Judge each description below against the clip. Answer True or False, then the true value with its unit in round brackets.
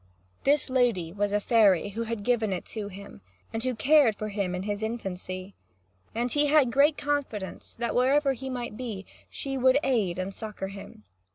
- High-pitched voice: True (225 Hz)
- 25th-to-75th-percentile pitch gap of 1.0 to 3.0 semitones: False (4.5 semitones)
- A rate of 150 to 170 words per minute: False (190 wpm)